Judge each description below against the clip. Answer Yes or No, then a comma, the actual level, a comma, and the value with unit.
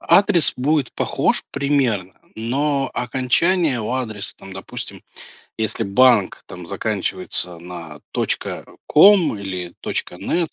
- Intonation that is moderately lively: No, wide, 7.3 semitones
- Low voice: Yes, low, 120 Hz